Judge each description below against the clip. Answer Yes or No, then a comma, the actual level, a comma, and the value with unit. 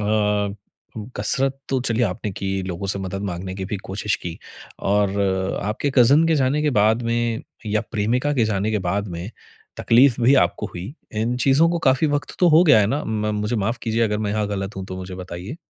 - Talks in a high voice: No, low, 110 Hz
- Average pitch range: Yes, average, 4.6 semitones